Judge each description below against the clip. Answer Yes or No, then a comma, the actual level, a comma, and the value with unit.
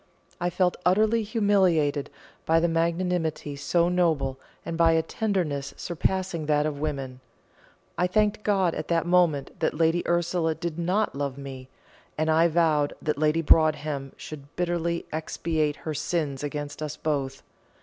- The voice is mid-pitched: Yes, medium, 160 Hz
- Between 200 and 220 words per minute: No, average, 150 wpm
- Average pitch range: Yes, average, 3.1 semitones